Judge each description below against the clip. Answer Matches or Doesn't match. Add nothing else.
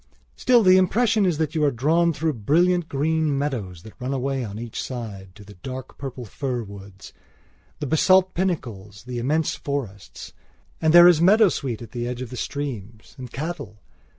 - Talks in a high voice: Doesn't match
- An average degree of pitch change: Doesn't match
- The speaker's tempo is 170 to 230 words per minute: Matches